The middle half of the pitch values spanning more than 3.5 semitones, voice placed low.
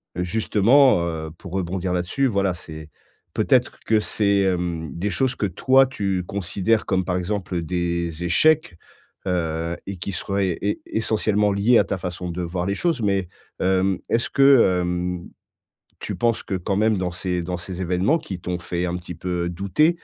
No: average, 2.9 semitones; very low, 95 Hz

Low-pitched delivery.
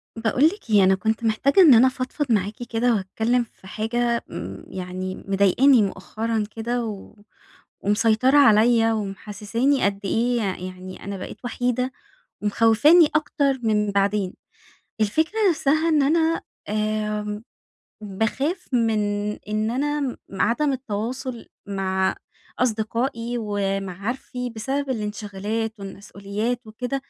No: high, 225 Hz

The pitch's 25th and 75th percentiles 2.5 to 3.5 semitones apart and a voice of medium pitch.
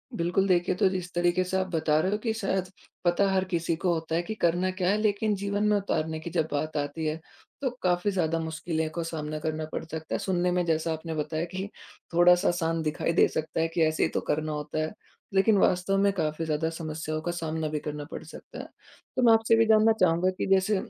Yes: average, 3.1 semitones; medium, 170 Hz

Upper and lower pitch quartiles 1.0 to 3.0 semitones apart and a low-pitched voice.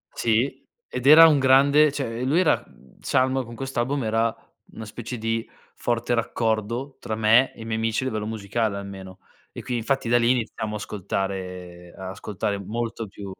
No: average, 3.7 semitones; low, 115 Hz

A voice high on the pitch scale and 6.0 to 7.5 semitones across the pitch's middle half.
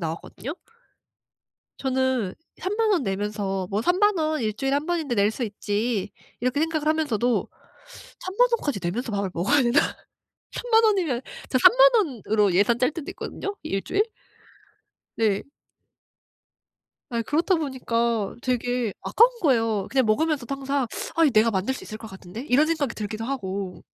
Yes: very high, 250 Hz; wide, 6.5 semitones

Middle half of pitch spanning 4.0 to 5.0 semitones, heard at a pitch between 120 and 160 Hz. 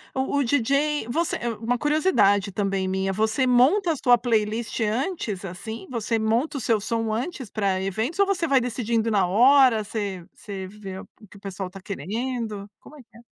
No: average, 4.7 semitones; high, 225 Hz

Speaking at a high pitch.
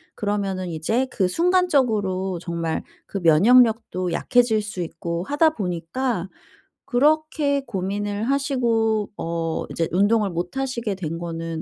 Yes: high, 205 Hz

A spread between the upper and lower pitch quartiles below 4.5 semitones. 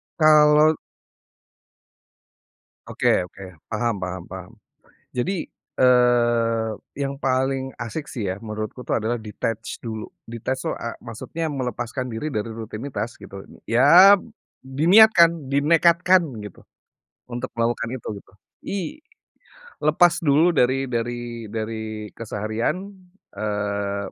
No: average, 4.8 semitones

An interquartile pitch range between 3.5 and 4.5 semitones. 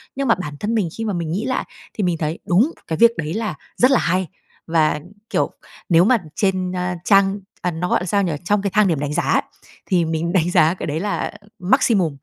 Yes: average, 3.9 semitones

